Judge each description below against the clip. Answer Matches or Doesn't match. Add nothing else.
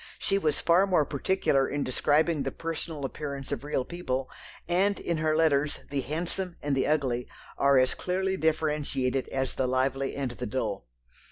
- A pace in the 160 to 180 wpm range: Matches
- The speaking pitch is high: Doesn't match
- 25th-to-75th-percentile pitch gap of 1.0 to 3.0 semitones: Doesn't match